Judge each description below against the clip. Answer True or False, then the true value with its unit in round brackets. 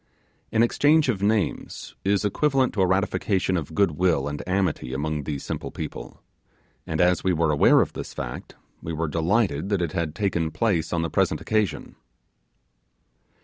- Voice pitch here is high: False (90 Hz)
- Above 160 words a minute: True (170 wpm)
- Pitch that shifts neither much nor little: True (4.2 semitones)